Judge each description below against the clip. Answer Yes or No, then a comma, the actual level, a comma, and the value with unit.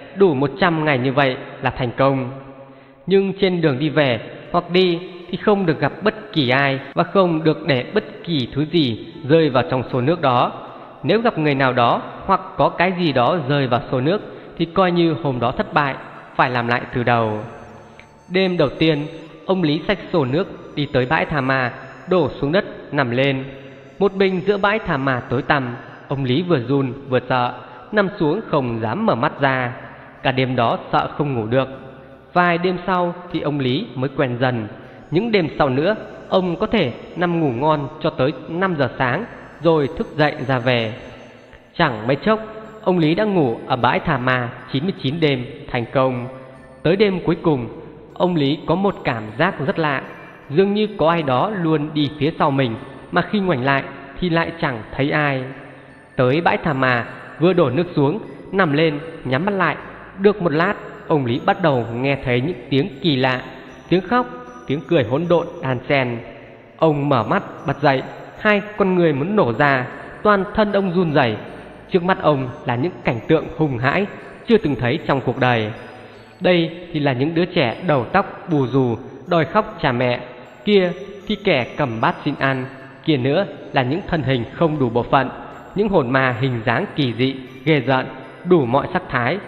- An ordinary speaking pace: Yes, average, 195 wpm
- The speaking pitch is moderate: Yes, medium, 145 Hz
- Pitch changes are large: No, average, 4.9 semitones